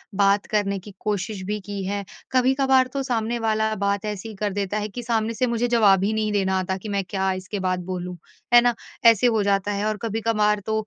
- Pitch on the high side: Yes, high, 210 Hz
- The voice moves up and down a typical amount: No, narrow, 2.3 semitones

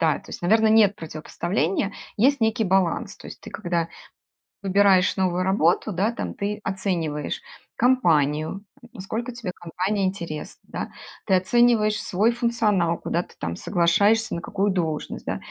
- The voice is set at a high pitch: Yes, high, 195 Hz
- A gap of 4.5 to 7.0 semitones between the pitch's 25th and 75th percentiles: No, average, 4.0 semitones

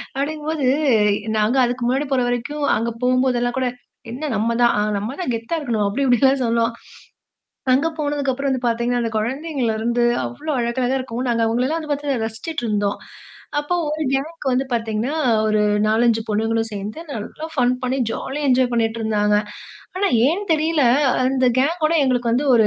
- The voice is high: Yes, very high, 250 Hz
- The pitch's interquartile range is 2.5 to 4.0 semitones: Yes, average, 3.7 semitones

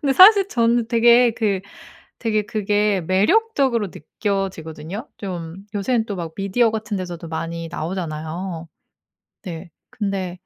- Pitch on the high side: Yes, high, 200 Hz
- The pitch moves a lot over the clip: No, average, 5.0 semitones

